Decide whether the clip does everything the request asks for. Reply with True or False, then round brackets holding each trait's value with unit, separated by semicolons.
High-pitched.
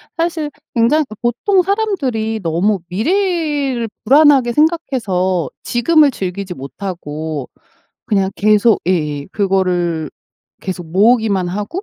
True (215 Hz)